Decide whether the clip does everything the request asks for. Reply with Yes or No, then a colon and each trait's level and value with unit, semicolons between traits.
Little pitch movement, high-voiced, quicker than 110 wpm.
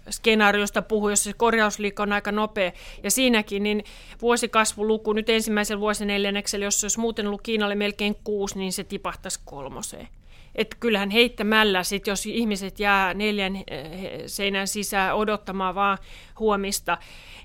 Yes: narrow, 1.4 semitones; high, 205 Hz; average, 140 wpm